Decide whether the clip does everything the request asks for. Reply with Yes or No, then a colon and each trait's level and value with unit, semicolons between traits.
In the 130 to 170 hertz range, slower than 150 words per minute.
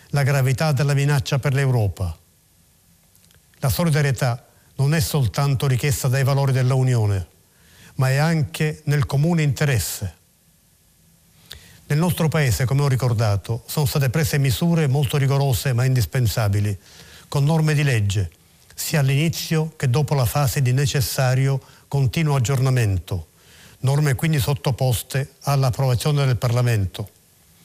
Yes: low, 135 Hz; average, 120 wpm